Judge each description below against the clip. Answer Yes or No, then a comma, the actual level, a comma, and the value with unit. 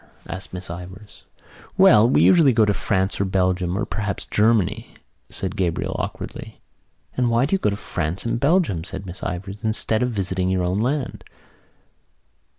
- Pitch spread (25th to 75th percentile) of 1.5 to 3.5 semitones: No, average, 3.9 semitones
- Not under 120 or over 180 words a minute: Yes, average, 165 wpm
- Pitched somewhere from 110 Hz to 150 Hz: No, low, 100 Hz